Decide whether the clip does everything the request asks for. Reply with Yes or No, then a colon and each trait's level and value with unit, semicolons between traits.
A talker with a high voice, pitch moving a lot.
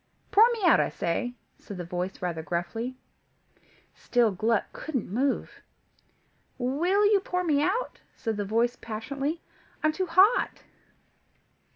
Yes: very high, 255 Hz; wide, 8.6 semitones